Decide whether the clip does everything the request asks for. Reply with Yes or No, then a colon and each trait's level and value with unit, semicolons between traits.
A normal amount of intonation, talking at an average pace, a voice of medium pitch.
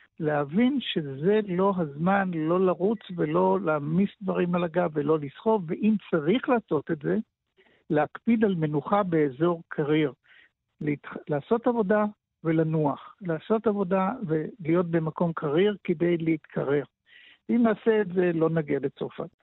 Yes: average, 4.9 semitones; average, 125 wpm; medium, 180 Hz